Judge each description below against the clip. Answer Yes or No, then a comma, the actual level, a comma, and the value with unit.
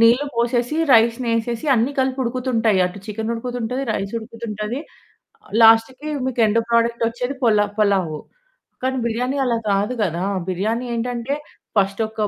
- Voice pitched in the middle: No, high, 230 Hz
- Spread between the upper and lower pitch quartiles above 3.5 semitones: No, narrow, 2.5 semitones